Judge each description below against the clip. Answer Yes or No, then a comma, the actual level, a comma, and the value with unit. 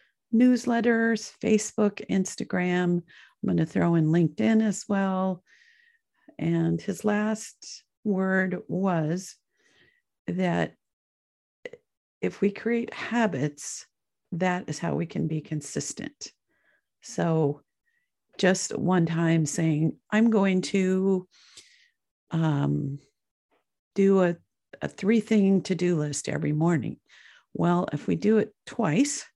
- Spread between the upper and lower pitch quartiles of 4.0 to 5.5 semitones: Yes, average, 4.8 semitones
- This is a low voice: No, high, 190 Hz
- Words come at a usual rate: No, slow, 110 wpm